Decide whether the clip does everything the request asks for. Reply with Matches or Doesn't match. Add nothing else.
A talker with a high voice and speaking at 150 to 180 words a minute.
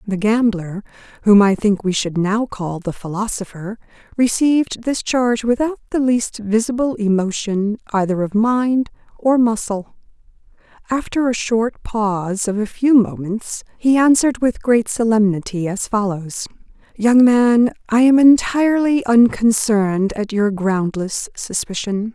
Doesn't match